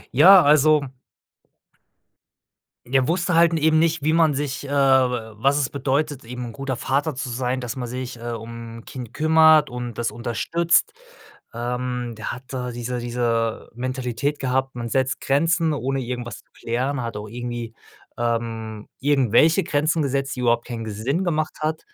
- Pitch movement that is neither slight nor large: Yes, average, 3.7 semitones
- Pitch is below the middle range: Yes, low, 130 Hz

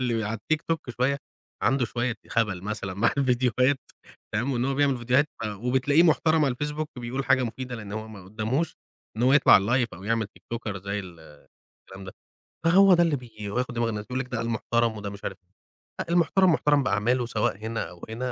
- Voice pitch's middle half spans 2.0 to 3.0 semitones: No, average, 4.1 semitones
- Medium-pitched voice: No, low, 120 Hz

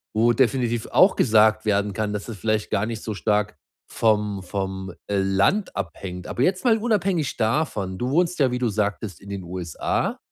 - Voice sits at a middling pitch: No, low, 110 Hz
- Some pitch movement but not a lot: Yes, average, 3.9 semitones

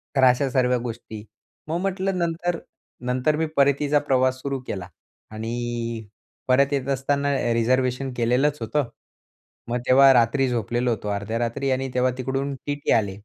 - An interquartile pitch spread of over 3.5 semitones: No, average, 2.9 semitones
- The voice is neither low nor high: No, low, 130 Hz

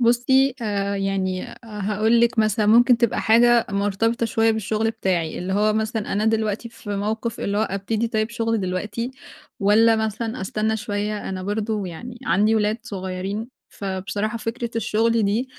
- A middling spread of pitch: No, narrow, 2.2 semitones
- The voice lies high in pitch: Yes, high, 215 Hz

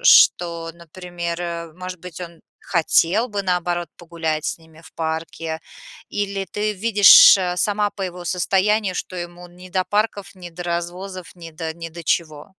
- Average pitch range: No, narrow, 2.2 semitones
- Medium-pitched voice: Yes, medium, 175 Hz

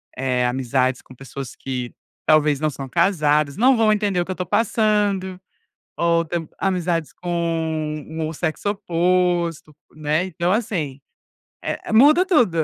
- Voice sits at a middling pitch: Yes, medium, 170 Hz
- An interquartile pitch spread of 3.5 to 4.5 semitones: Yes, average, 4.1 semitones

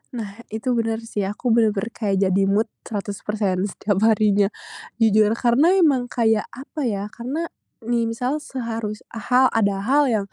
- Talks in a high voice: Yes, high, 225 Hz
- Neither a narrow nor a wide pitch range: Yes, average, 3.0 semitones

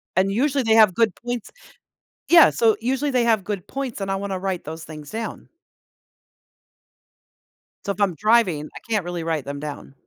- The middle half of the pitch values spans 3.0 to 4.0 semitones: No, average, 5.0 semitones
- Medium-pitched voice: No, high, 200 Hz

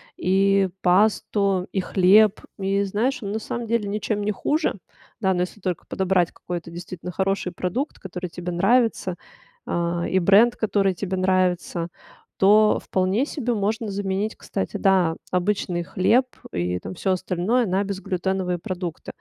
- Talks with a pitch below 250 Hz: Yes, high, 190 Hz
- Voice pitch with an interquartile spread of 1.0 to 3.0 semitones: Yes, narrow, 2.6 semitones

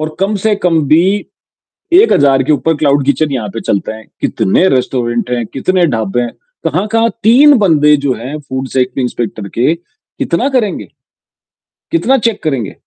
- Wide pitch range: Yes, wide, 7.2 semitones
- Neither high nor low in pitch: Yes, medium, 145 Hz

